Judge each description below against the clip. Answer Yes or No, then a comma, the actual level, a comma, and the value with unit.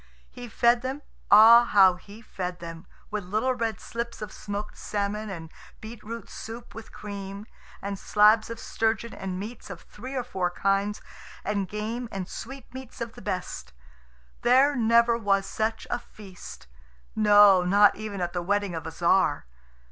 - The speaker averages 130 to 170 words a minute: Yes, average, 160 wpm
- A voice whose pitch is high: Yes, high, 210 Hz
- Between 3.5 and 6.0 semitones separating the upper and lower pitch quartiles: No, average, 3.1 semitones